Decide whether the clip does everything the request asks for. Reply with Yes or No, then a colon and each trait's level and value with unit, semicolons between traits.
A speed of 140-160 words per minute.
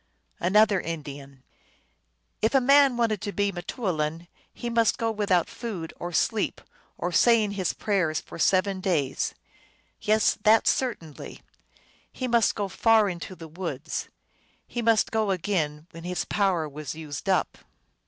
Yes: average, 150 wpm